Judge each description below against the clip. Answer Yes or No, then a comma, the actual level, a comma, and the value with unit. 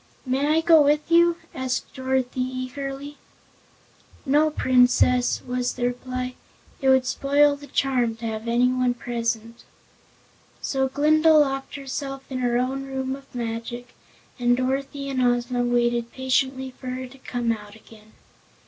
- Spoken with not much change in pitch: Yes, narrow, 1.9 semitones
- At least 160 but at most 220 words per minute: No, average, 140 wpm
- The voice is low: No, very high, 255 Hz